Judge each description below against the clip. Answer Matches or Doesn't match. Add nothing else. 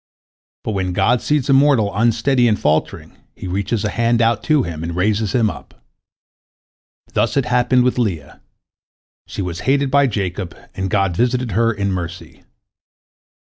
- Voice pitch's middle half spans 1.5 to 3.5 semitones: Doesn't match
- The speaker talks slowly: Doesn't match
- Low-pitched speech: Matches